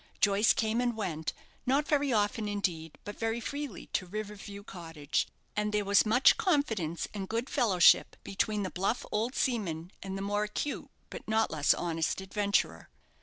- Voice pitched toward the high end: Yes, high, 205 Hz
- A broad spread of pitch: No, average, 3.1 semitones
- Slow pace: No, average, 170 wpm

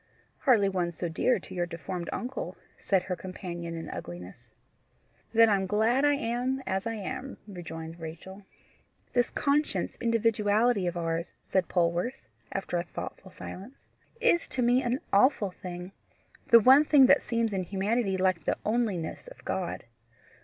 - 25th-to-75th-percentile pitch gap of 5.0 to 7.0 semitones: Yes, wide, 5.5 semitones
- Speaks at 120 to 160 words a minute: Yes, average, 155 wpm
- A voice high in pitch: Yes, high, 195 Hz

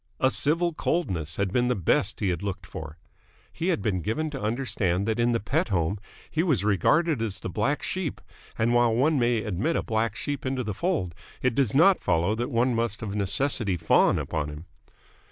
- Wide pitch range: Yes, wide, 5.7 semitones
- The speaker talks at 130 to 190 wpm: No, fast, 205 wpm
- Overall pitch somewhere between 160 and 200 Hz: No, low, 115 Hz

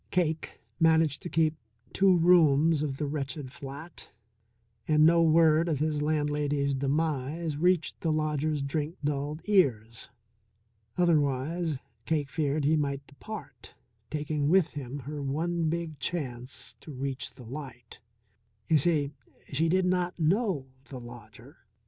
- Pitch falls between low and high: Yes, medium, 150 Hz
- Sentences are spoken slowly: Yes, slow, 130 wpm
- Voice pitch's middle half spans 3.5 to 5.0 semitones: No, average, 2.8 semitones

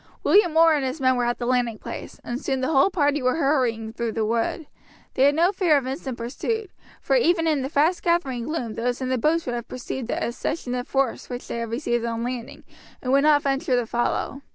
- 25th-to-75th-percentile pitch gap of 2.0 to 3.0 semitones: No, average, 4.1 semitones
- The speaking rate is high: Yes, fast, 235 wpm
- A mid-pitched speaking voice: No, very high, 260 Hz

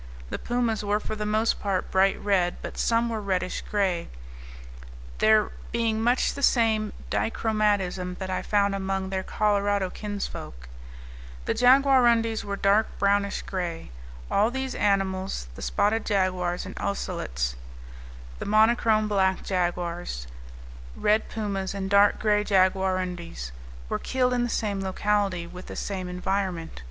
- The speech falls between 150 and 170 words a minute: No, slow, 135 wpm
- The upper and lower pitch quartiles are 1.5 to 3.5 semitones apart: Yes, narrow, 2.6 semitones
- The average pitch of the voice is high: Yes, high, 200 Hz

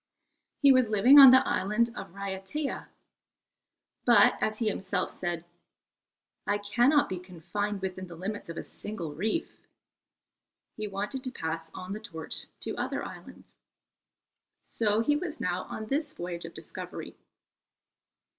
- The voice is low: No, high, 205 Hz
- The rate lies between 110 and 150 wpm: Yes, average, 140 wpm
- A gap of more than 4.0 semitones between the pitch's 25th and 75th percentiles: Yes, average, 4.6 semitones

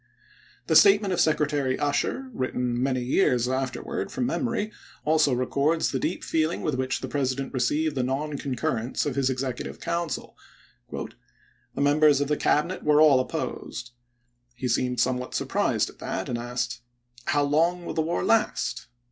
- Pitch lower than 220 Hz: Yes, medium, 140 Hz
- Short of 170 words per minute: Yes, average, 160 wpm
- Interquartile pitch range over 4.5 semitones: No, average, 3.7 semitones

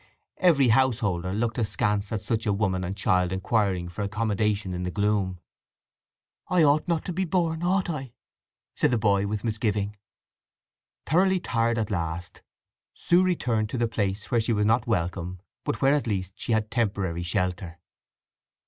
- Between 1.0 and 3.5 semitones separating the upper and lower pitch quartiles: No, average, 4.2 semitones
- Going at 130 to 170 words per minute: Yes, average, 165 wpm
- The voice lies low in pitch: Yes, low, 105 Hz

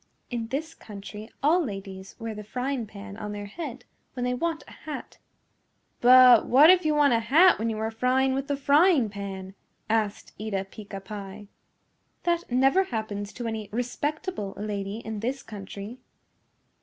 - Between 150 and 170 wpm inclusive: Yes, average, 165 wpm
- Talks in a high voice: Yes, high, 225 Hz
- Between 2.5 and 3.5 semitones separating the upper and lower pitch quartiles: No, average, 4.8 semitones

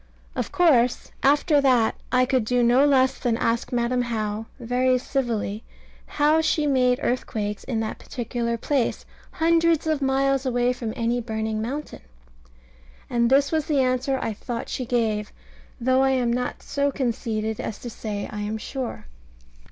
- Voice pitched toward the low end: No, high, 245 Hz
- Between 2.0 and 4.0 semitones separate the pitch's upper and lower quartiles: Yes, average, 2.8 semitones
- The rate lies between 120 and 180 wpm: Yes, average, 160 wpm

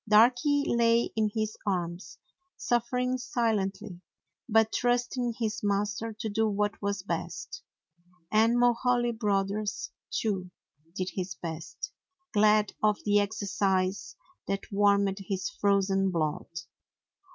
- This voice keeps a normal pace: No, slow, 115 wpm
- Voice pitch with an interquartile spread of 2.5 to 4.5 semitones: Yes, average, 2.8 semitones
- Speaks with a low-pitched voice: No, high, 210 Hz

